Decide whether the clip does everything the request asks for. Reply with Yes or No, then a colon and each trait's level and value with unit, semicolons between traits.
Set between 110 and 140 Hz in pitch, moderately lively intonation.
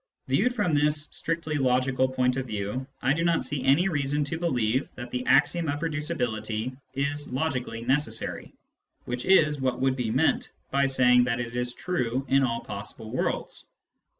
Yes: low, 135 Hz; average, 3.2 semitones